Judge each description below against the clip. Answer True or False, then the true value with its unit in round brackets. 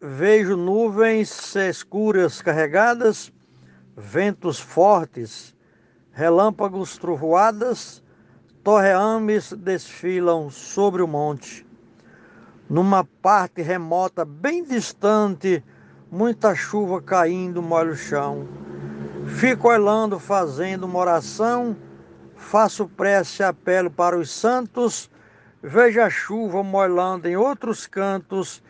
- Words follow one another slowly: True (90 wpm)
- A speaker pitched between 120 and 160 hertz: False (185 Hz)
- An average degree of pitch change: True (4.5 semitones)